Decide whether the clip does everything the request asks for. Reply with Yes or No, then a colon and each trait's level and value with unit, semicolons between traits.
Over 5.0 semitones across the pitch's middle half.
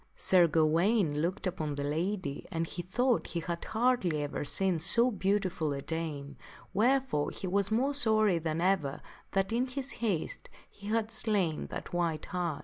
Yes: wide, 5.4 semitones